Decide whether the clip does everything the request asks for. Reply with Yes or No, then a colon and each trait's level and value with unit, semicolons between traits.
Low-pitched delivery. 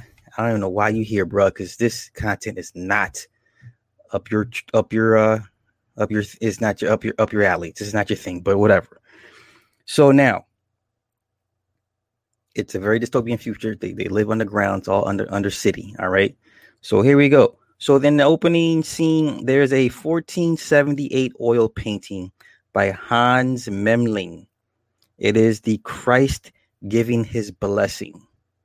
Yes: low, 110 Hz